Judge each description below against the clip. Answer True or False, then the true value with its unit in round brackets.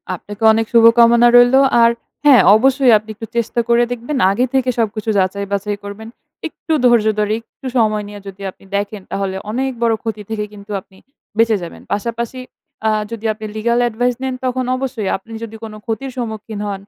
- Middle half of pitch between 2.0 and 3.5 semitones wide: True (2.5 semitones)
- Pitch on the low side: False (225 Hz)